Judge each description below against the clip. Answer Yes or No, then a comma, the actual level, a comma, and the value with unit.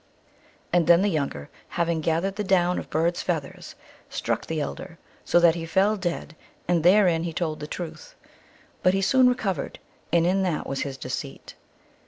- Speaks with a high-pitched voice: No, medium, 170 Hz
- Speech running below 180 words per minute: No, average, 185 wpm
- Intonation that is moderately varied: Yes, average, 3.0 semitones